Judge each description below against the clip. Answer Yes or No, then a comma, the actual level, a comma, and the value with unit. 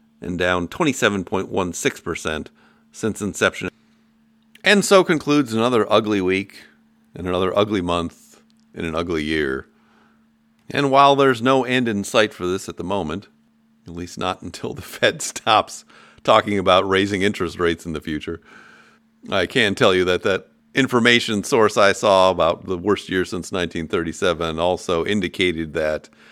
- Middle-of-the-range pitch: No, low, 100 Hz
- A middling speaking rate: Yes, average, 150 wpm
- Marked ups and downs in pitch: Yes, wide, 8.8 semitones